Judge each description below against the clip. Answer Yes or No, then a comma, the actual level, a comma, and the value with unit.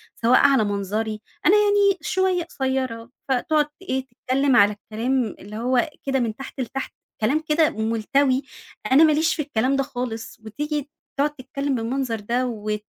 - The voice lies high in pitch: Yes, very high, 260 Hz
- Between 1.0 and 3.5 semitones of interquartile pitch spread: No, average, 4.2 semitones